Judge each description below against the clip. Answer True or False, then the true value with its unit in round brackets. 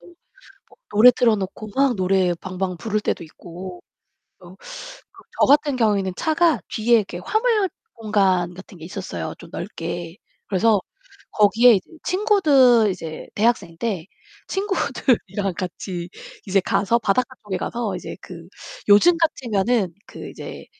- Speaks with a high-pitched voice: True (210 Hz)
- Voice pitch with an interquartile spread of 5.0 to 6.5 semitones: True (5.3 semitones)